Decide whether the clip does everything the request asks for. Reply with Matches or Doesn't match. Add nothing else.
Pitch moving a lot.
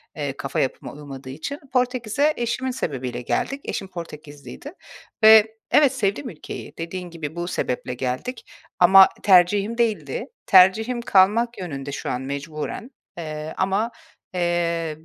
Matches